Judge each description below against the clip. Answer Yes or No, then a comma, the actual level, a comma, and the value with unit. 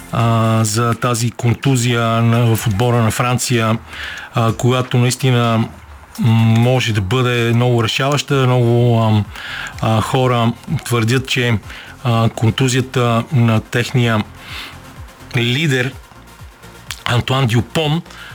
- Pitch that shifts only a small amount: Yes, narrow, 2.1 semitones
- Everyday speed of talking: No, slow, 80 wpm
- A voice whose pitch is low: Yes, low, 120 Hz